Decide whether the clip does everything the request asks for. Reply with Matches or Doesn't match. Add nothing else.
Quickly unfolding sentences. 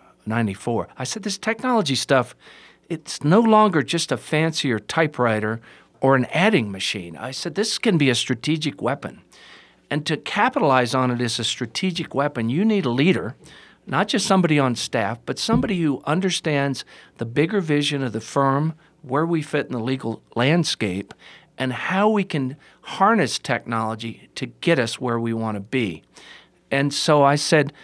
Doesn't match